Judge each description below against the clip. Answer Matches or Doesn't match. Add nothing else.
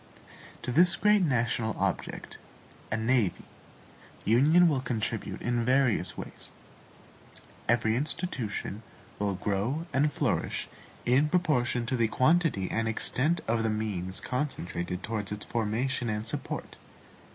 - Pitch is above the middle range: Doesn't match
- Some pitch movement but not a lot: Matches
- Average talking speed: Doesn't match